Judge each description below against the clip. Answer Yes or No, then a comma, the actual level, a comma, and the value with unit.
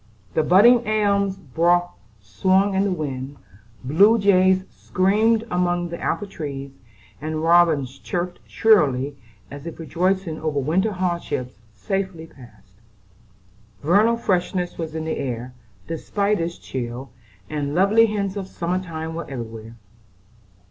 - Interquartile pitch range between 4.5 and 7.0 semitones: Yes, average, 5.3 semitones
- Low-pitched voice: No, medium, 175 Hz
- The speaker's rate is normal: No, slow, 130 wpm